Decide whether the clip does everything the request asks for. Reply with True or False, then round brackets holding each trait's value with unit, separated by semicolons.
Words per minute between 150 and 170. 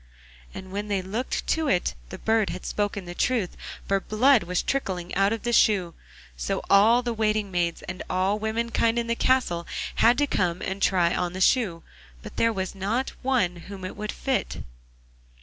False (190 wpm)